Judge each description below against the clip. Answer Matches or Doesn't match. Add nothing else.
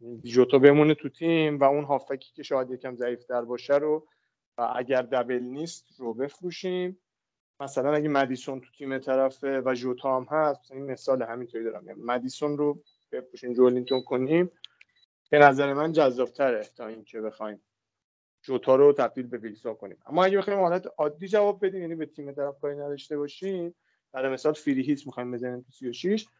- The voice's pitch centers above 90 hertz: Matches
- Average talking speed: Doesn't match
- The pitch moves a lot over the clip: Doesn't match